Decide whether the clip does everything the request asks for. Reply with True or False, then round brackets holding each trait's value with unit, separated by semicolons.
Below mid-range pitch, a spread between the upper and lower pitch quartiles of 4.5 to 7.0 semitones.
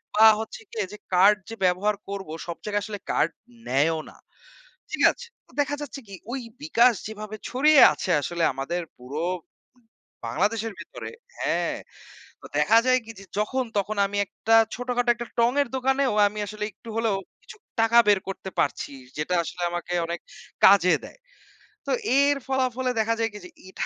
False (215 Hz; 5.0 semitones)